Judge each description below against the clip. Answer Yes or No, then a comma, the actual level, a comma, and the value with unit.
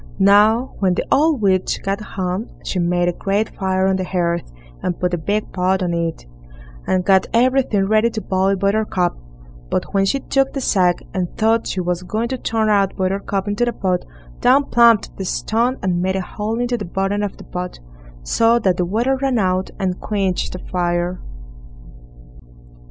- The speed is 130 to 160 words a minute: No, average, 185 wpm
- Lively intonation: No, average, 3.5 semitones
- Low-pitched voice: No, high, 195 Hz